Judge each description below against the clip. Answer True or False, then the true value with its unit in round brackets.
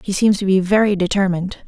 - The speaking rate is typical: False (215 wpm)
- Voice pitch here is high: True (195 Hz)